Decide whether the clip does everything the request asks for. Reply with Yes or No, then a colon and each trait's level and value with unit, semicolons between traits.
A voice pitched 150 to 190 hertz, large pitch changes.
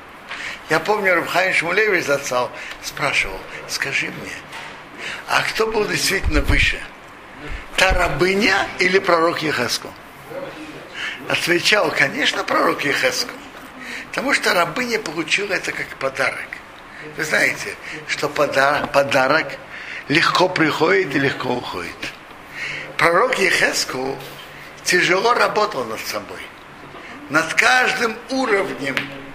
No: medium, 185 Hz; average, 4.3 semitones